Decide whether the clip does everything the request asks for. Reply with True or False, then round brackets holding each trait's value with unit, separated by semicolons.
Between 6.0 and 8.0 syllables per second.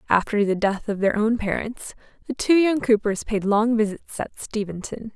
False (4.8 syllables/s)